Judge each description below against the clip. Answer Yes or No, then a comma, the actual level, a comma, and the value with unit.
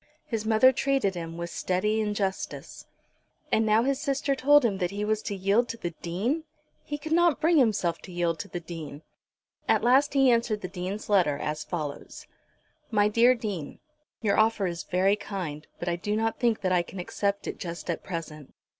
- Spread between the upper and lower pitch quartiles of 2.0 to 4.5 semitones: No, average, 5.0 semitones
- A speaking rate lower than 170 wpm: No, average, 195 wpm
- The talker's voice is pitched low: No, high, 205 Hz